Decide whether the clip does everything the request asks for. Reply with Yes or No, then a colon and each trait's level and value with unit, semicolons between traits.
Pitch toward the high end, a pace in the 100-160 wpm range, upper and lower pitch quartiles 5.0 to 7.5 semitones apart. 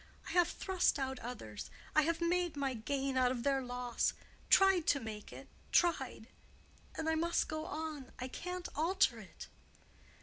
Yes: very high, 280 Hz; average, 145 wpm; average, 5.3 semitones